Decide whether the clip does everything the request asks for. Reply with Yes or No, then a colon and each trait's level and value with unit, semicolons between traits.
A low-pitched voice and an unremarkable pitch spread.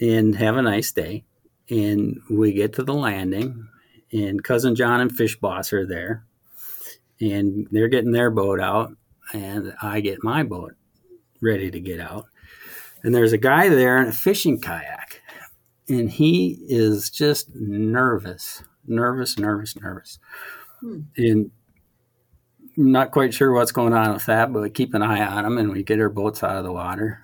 Yes: low, 110 Hz; average, 3.1 semitones